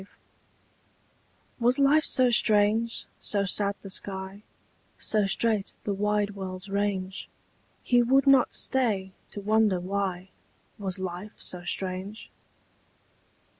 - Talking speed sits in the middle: No, slow, 115 wpm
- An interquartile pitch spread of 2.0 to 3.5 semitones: Yes, average, 2.7 semitones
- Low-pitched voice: No, high, 205 Hz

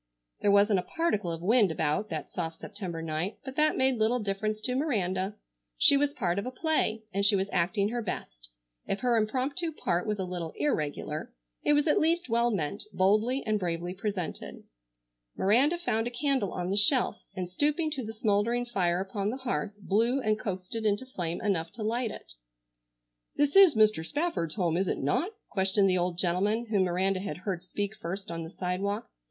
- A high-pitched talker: Yes, high, 205 Hz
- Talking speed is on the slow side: No, average, 195 wpm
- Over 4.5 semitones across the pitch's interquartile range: Yes, average, 5.0 semitones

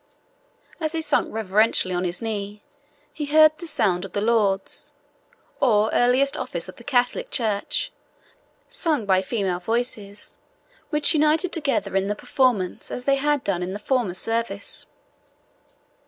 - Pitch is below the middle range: No, high, 225 Hz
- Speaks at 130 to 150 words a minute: Yes, average, 145 wpm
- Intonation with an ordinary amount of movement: No, wide, 5.9 semitones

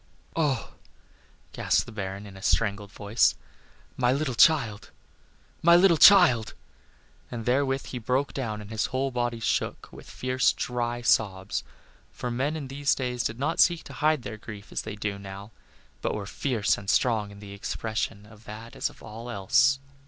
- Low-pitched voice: Yes, low, 115 Hz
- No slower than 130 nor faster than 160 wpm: No, average, 175 wpm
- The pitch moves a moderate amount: Yes, average, 4.2 semitones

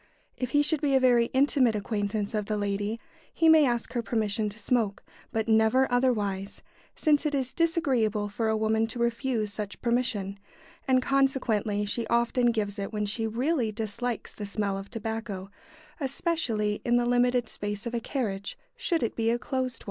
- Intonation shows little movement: No, average, 3.4 semitones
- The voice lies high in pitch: Yes, high, 230 Hz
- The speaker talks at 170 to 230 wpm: Yes, average, 180 wpm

